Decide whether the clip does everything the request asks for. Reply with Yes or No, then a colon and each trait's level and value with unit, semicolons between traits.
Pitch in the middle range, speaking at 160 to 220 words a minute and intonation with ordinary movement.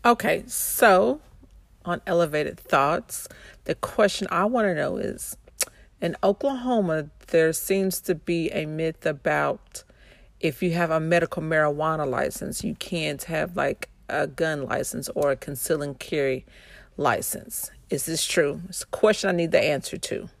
No: medium, 165 Hz; average, 150 wpm; average, 3.3 semitones